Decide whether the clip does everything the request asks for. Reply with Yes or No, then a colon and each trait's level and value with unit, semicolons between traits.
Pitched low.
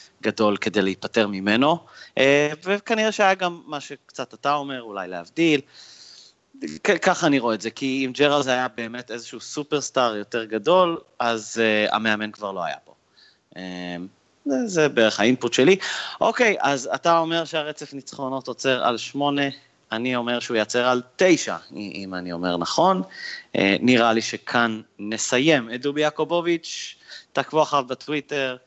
Yes: low, 125 Hz